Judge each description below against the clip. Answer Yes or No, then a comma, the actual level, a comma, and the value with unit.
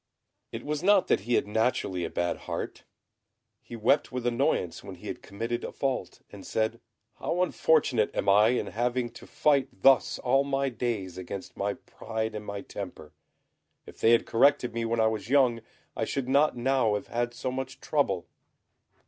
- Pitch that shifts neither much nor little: Yes, average, 3.9 semitones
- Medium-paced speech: Yes, average, 180 wpm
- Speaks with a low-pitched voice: Yes, low, 120 Hz